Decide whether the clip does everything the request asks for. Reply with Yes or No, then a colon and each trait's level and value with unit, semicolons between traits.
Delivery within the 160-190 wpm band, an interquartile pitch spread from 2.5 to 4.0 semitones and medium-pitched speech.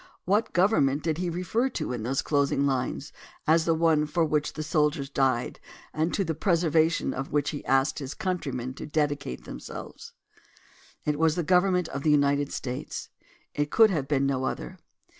Yes: average, 180 wpm; average, 3.4 semitones; medium, 150 Hz